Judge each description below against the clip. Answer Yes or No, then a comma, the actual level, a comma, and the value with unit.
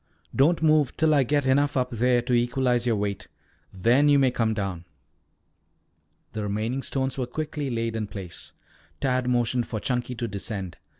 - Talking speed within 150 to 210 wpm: Yes, average, 170 wpm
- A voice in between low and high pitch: No, low, 125 Hz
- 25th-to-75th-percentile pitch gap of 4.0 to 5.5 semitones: No, average, 3.3 semitones